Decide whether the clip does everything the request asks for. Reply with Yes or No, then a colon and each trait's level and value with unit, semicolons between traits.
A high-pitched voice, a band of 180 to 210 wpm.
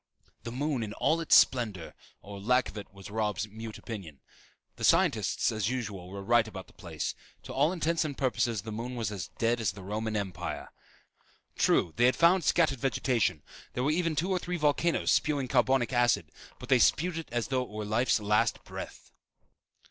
No: low, 120 Hz; average, 195 wpm